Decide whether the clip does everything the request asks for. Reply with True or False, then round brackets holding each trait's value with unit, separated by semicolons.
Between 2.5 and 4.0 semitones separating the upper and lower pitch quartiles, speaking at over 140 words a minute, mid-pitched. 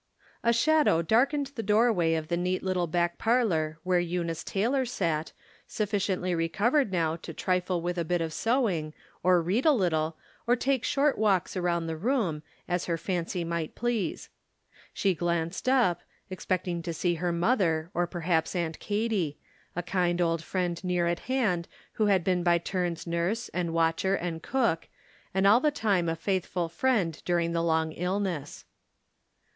True (3.7 semitones; 175 wpm; 180 Hz)